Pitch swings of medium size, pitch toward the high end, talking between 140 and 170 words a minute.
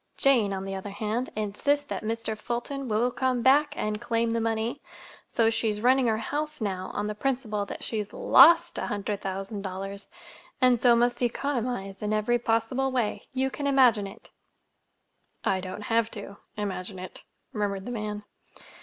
Yes: average, 3.5 semitones; high, 225 Hz; average, 165 wpm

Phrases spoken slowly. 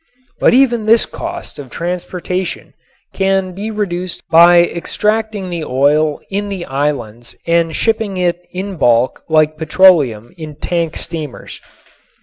Yes: slow, 130 wpm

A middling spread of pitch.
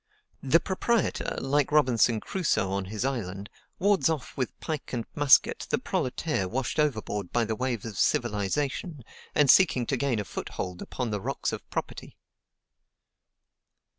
No: wide, 5.8 semitones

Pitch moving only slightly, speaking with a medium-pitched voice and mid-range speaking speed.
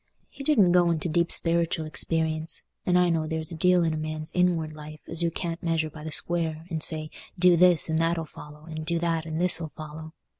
No: narrow, 1.6 semitones; medium, 165 Hz; fast, 235 wpm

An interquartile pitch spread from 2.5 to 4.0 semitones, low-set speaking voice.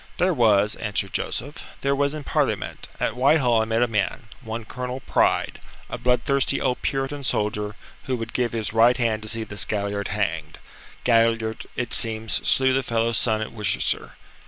Yes: average, 2.8 semitones; low, 115 Hz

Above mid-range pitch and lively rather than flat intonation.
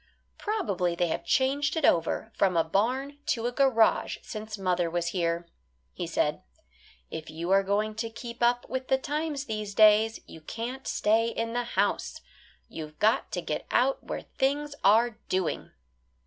Yes: high, 220 Hz; wide, 5.9 semitones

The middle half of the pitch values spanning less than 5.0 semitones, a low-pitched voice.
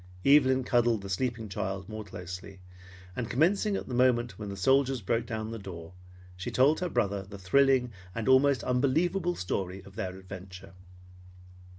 No: average, 5.3 semitones; low, 115 Hz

